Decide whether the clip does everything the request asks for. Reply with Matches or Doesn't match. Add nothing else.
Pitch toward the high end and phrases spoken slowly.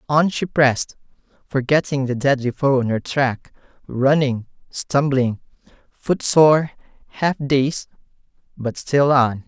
Doesn't match